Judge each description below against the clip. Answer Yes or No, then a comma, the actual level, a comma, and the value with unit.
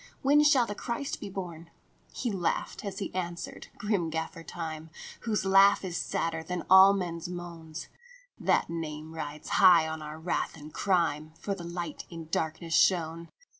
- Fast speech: No, average, 175 wpm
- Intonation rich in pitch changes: No, average, 3.3 semitones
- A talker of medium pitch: Yes, medium, 170 Hz